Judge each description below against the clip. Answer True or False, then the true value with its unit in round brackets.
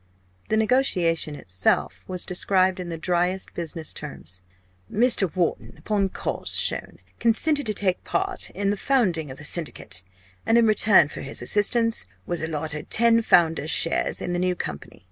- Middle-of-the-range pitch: True (180 Hz)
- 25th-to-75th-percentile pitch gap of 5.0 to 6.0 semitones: True (5.3 semitones)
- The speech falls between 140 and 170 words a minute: True (160 wpm)